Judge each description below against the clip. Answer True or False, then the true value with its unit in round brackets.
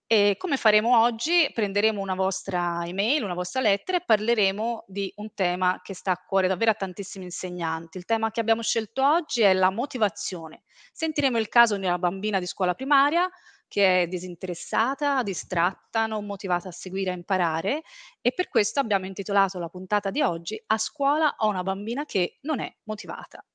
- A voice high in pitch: True (205 Hz)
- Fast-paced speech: True (180 wpm)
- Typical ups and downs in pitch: True (4.3 semitones)